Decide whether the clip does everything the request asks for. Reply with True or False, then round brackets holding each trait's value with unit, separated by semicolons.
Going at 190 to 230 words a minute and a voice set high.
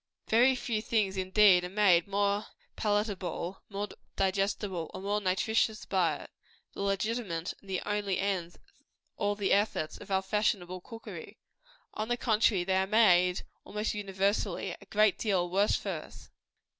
False (150 wpm; 200 Hz)